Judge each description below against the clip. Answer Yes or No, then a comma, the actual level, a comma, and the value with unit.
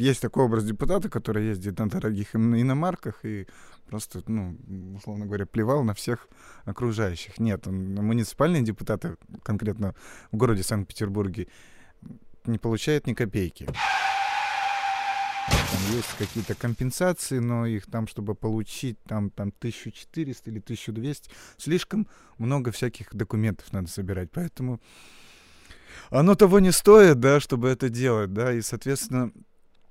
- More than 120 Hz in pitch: No, low, 115 Hz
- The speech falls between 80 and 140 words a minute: Yes, average, 120 wpm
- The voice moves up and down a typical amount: Yes, average, 4.3 semitones